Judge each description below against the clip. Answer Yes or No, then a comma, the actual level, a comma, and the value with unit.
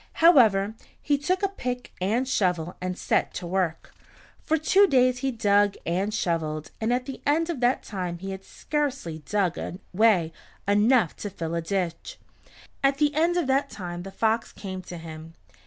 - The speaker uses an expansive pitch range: Yes, wide, 7.0 semitones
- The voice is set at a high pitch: Yes, high, 205 Hz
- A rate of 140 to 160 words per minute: No, average, 175 wpm